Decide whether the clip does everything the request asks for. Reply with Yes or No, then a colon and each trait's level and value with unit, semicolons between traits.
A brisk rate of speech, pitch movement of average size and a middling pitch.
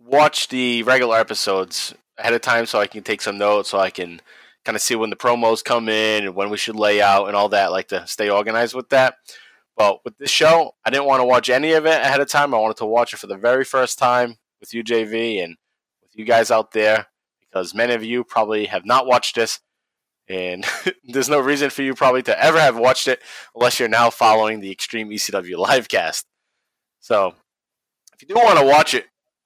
No: fast, 225 wpm; average, 3.5 semitones; low, 115 Hz